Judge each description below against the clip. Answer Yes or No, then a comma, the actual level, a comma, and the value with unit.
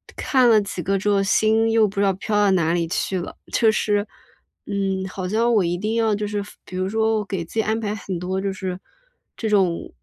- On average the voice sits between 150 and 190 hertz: No, high, 200 Hz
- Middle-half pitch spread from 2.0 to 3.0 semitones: Yes, narrow, 2.5 semitones